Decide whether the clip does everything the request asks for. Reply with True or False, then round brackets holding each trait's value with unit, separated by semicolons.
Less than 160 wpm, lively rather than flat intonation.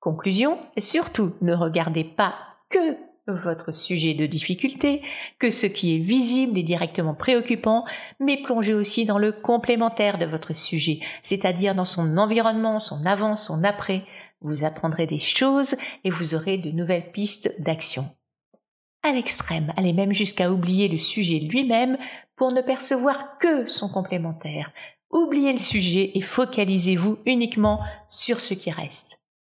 True (145 wpm; 6.4 semitones)